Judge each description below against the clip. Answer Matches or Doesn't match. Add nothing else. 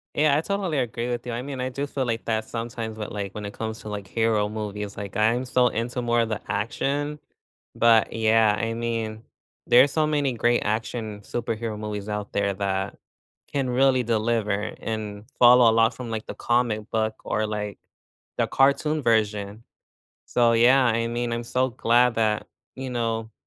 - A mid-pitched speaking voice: Doesn't match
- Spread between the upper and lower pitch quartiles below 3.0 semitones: Matches